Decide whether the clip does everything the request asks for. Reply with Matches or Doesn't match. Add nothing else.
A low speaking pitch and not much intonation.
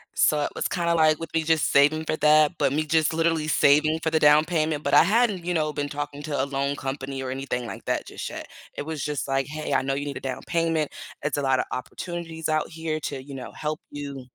Doesn't match